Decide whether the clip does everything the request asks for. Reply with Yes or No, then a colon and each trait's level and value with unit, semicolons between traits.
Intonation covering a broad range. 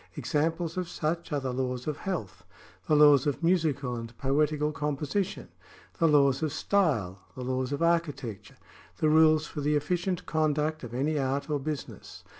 No: average, 3.0 semitones